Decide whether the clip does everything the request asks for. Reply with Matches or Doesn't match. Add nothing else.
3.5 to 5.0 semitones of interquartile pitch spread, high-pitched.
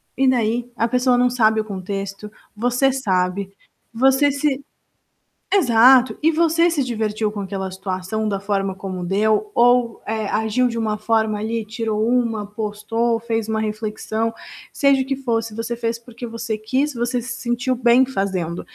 Doesn't match